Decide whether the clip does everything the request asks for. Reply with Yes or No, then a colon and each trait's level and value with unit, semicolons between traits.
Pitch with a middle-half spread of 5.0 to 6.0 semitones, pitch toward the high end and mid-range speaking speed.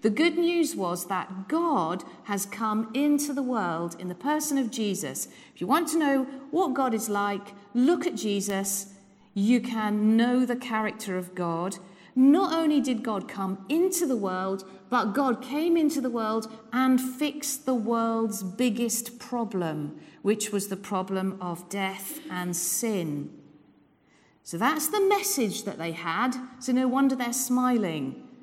Yes: wide, 5.6 semitones; high, 225 Hz; average, 160 wpm